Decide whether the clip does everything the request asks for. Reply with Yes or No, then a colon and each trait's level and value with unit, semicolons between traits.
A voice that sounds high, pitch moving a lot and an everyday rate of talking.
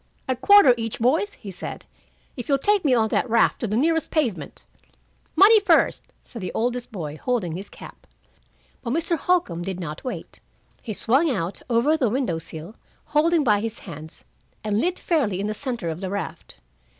Yes: high, 235 Hz; wide, 7.4 semitones; average, 185 wpm